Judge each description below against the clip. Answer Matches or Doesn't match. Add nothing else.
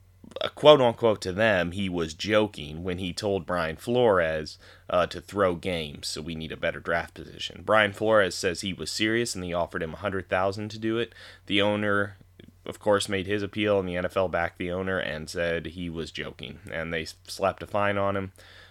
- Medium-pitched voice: Doesn't match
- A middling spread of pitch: Matches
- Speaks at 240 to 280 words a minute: Doesn't match